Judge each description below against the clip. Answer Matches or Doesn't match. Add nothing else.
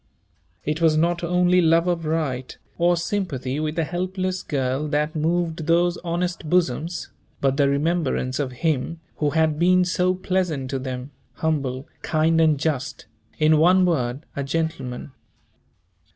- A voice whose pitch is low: Doesn't match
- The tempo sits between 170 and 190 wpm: Doesn't match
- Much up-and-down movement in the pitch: Doesn't match